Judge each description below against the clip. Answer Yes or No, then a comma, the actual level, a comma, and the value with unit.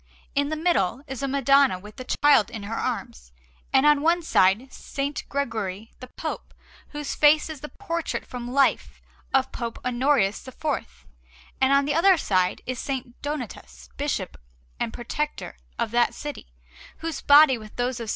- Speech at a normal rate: Yes, average, 170 wpm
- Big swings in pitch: No, average, 4.5 semitones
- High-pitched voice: Yes, very high, 265 Hz